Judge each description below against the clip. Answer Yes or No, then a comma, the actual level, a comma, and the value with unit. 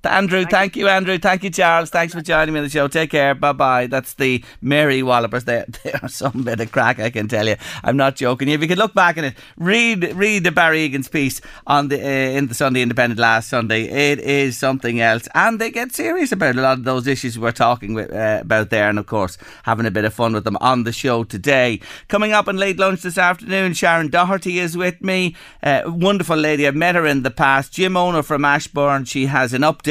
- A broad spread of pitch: Yes, wide, 6.2 semitones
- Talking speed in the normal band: No, fast, 240 wpm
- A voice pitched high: No, medium, 140 Hz